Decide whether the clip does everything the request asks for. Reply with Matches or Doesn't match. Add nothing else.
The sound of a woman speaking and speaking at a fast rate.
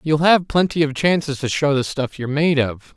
Doesn't match